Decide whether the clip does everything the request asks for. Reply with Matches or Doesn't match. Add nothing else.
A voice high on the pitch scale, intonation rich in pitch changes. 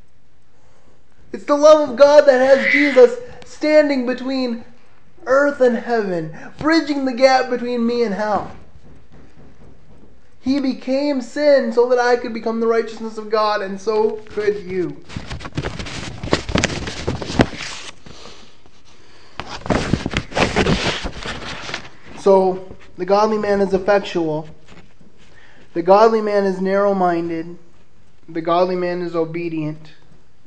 Matches